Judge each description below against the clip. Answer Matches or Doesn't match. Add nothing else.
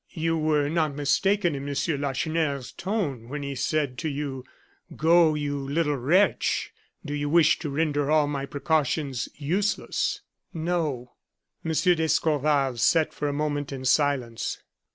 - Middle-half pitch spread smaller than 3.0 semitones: Matches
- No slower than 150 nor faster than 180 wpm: Doesn't match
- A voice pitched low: Doesn't match